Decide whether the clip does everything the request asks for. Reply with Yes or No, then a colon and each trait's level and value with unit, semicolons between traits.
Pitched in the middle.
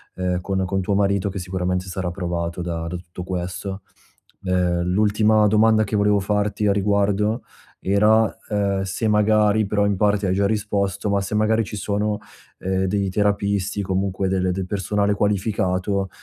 No: low, 100 Hz